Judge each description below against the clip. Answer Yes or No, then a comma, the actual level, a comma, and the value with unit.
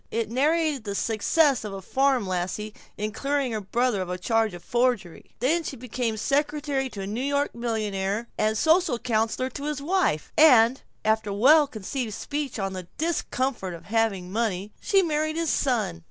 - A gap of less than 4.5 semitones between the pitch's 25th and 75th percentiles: No, wide, 5.5 semitones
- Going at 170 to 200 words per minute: Yes, average, 175 wpm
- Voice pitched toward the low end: No, high, 235 Hz